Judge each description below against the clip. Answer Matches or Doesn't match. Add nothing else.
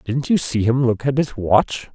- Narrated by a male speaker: Matches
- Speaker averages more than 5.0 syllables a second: Doesn't match